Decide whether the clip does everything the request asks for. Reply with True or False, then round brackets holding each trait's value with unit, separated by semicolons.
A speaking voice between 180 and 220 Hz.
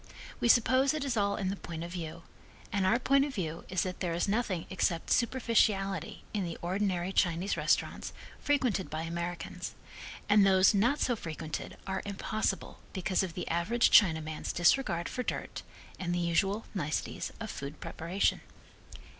True (190 Hz)